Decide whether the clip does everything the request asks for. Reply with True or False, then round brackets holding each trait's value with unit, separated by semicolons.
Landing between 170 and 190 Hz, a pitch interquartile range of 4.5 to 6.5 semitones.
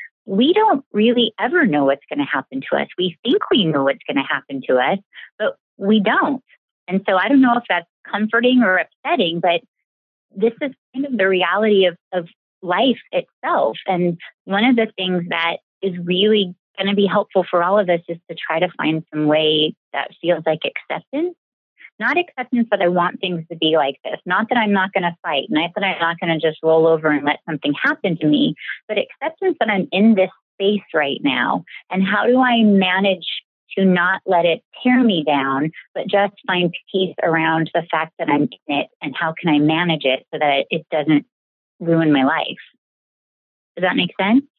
True (185 Hz; 5.1 semitones)